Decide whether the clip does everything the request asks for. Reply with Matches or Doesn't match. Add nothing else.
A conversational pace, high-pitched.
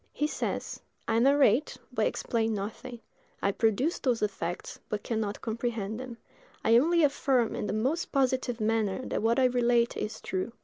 Matches